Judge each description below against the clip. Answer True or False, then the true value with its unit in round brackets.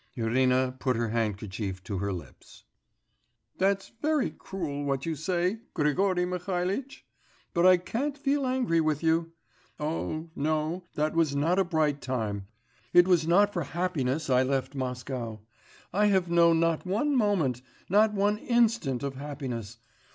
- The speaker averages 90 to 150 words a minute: True (145 wpm)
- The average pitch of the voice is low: False (160 Hz)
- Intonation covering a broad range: True (6.3 semitones)